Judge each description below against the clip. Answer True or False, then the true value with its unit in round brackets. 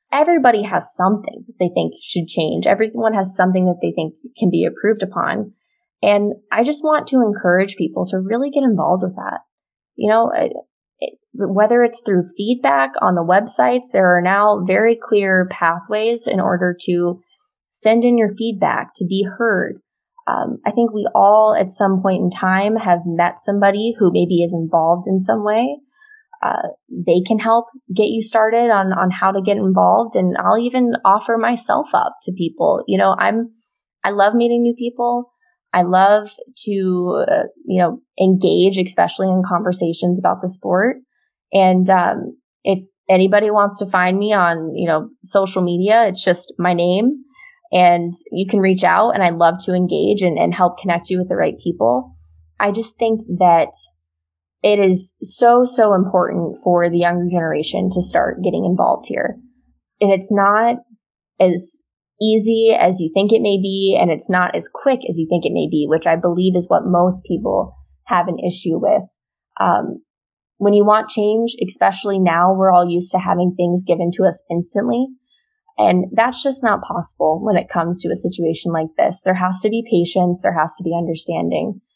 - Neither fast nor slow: True (180 wpm)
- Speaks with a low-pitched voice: False (195 Hz)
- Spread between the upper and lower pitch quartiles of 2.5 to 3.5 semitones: False (4.2 semitones)